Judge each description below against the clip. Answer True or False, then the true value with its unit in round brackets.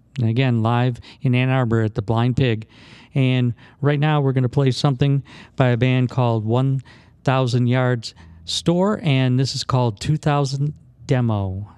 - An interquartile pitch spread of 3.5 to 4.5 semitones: False (2.5 semitones)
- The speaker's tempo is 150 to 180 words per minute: True (160 wpm)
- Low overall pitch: True (125 Hz)